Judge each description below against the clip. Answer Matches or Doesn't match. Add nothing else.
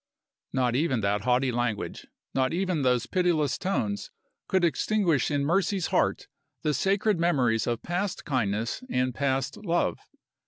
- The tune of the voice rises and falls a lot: Matches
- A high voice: Doesn't match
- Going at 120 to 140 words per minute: Matches